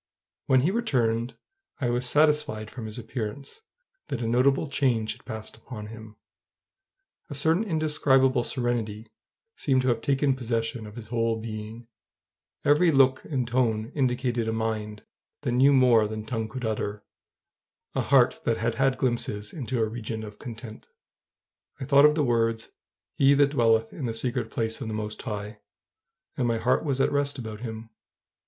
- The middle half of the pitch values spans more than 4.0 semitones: No, average, 3.2 semitones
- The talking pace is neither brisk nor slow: Yes, average, 165 wpm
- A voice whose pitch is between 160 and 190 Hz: No, low, 120 Hz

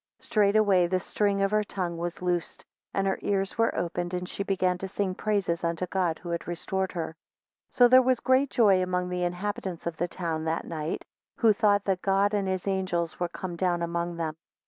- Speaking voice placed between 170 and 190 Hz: Yes, medium, 185 Hz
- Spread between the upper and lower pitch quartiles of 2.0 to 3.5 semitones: Yes, narrow, 2.6 semitones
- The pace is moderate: No, fast, 215 wpm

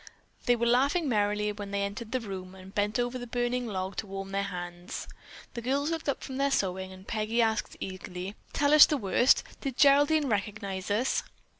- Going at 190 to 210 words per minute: Yes, average, 195 wpm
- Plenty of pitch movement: No, average, 4.6 semitones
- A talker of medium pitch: No, high, 215 Hz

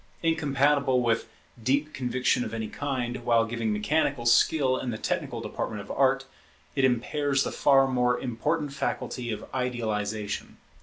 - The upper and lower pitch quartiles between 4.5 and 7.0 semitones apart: No, average, 3.0 semitones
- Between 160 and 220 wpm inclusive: No, average, 145 wpm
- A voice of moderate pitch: No, low, 125 Hz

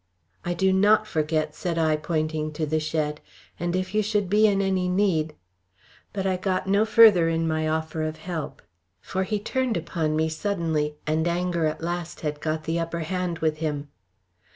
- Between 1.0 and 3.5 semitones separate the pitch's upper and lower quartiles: Yes, average, 3.2 semitones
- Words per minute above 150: Yes, average, 190 wpm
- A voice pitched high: No, medium, 165 Hz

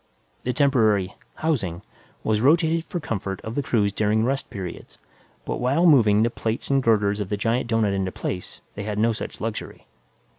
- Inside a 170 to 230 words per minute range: Yes, average, 180 wpm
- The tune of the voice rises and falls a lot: No, average, 4.3 semitones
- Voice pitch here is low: Yes, low, 110 Hz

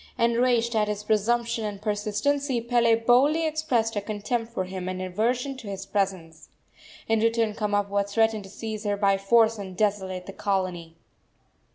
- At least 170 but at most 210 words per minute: No, average, 160 wpm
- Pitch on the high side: Yes, high, 215 Hz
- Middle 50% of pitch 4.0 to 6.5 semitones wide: No, average, 2.9 semitones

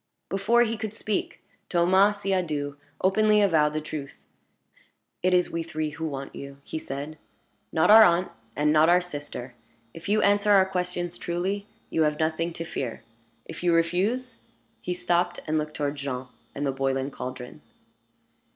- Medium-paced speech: Yes, average, 165 wpm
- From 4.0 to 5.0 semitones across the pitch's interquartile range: Yes, average, 4.3 semitones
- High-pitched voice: No, medium, 170 Hz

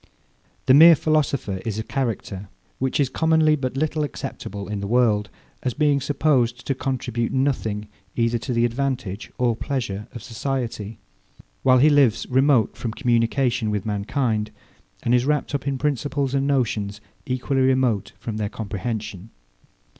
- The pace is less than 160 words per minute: Yes, average, 150 wpm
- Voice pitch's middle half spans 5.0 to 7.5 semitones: No, average, 3.9 semitones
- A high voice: No, low, 125 Hz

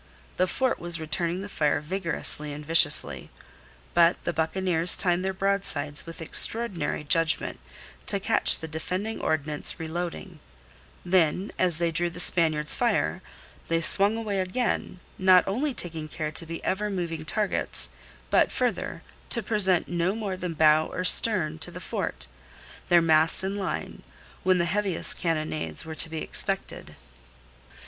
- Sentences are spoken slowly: No, average, 150 wpm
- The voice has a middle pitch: Yes, medium, 170 Hz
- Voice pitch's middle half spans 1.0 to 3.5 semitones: Yes, average, 3.1 semitones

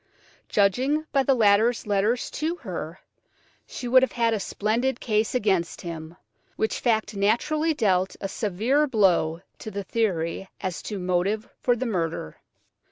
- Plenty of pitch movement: No, average, 4.4 semitones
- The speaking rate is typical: Yes, average, 150 wpm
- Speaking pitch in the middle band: No, high, 215 Hz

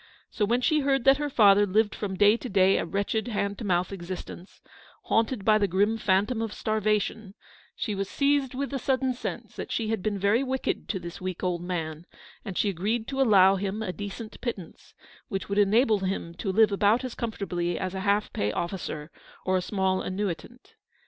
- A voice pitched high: Yes, high, 205 Hz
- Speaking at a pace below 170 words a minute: No, fast, 205 wpm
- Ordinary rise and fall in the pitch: Yes, average, 3.1 semitones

